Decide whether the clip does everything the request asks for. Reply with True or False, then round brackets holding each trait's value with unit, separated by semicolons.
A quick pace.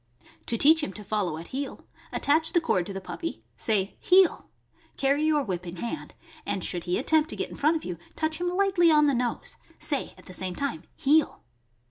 True (210 wpm)